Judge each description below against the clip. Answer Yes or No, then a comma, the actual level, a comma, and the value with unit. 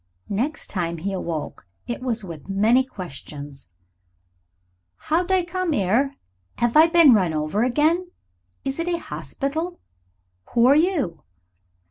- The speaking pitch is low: No, high, 245 Hz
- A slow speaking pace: Yes, slow, 130 wpm